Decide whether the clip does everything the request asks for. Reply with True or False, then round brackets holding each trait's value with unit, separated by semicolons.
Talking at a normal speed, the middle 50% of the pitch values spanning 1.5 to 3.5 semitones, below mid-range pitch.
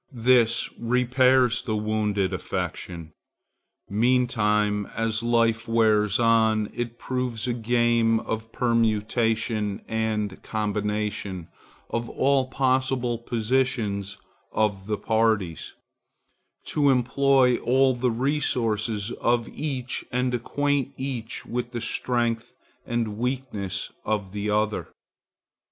False (100 wpm; 2.8 semitones; 115 Hz)